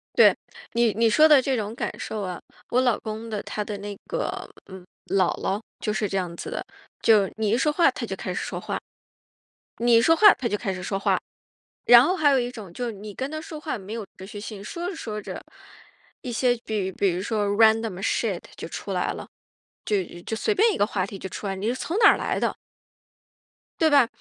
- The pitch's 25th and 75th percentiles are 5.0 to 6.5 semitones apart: No, average, 4.2 semitones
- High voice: Yes, high, 220 Hz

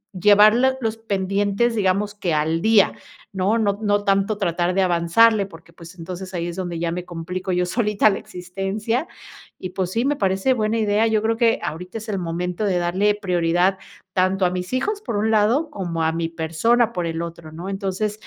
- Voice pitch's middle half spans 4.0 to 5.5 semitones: No, average, 3.4 semitones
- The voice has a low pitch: No, high, 195 Hz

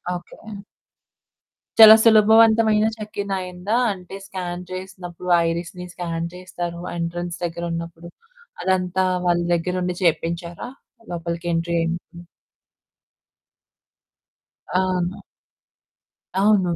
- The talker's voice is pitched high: No, medium, 180 Hz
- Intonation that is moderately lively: No, narrow, 1.7 semitones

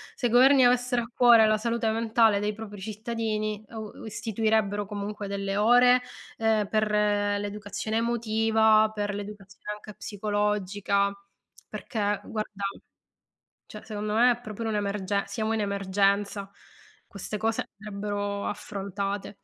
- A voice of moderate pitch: No, high, 210 Hz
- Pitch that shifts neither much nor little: No, narrow, 1.6 semitones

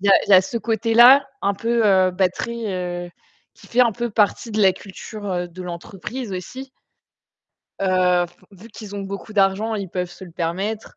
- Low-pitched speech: No, high, 200 Hz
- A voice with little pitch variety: No, average, 3.6 semitones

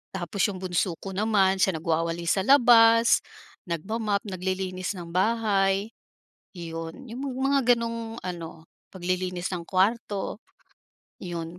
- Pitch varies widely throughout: No, average, 4.3 semitones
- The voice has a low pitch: No, high, 190 Hz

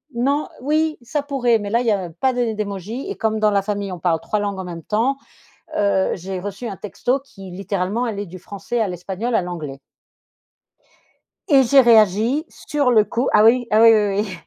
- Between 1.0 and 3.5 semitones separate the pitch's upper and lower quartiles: No, average, 4.1 semitones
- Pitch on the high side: Yes, high, 210 Hz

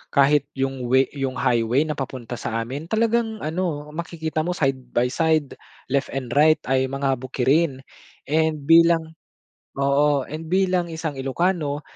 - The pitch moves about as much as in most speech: Yes, average, 3.3 semitones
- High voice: No, medium, 145 Hz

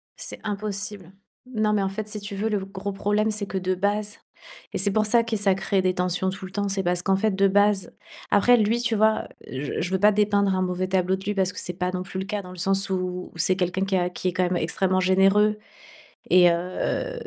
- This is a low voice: No, high, 195 Hz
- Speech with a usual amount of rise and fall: No, narrow, 2.1 semitones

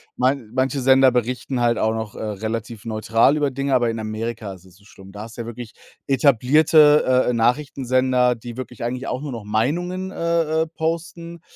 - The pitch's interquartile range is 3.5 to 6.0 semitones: Yes, average, 4.0 semitones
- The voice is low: Yes, low, 125 Hz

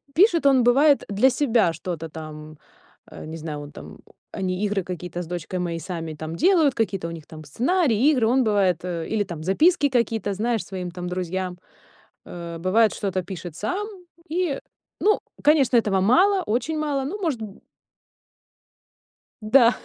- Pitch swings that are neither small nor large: No, wide, 7.5 semitones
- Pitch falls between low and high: No, high, 205 Hz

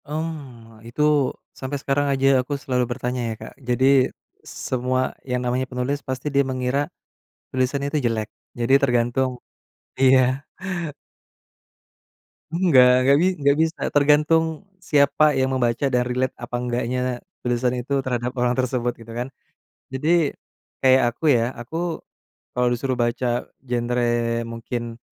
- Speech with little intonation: Yes, narrow, 2.3 semitones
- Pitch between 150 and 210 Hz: No, low, 130 Hz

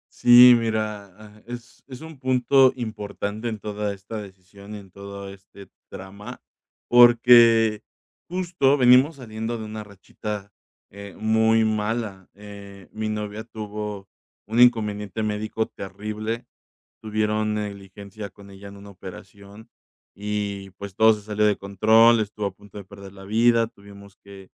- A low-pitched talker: Yes, low, 105 Hz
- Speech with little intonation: Yes, narrow, 2.0 semitones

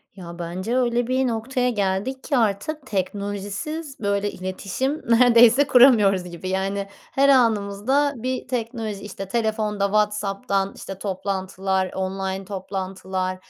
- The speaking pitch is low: No, high, 205 Hz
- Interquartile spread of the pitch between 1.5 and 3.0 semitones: No, average, 4.2 semitones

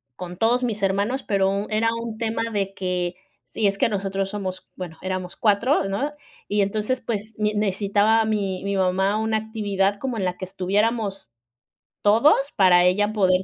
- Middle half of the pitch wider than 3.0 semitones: No, narrow, 2.4 semitones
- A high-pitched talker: Yes, high, 200 Hz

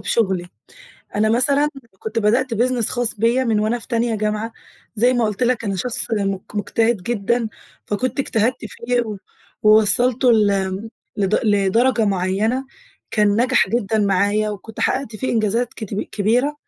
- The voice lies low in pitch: No, high, 220 Hz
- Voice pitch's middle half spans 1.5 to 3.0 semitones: Yes, average, 2.7 semitones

